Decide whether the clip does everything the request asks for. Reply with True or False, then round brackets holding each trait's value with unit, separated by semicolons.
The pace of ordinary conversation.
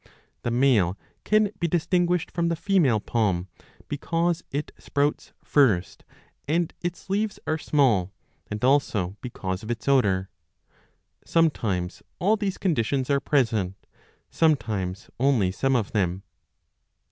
False (125 wpm)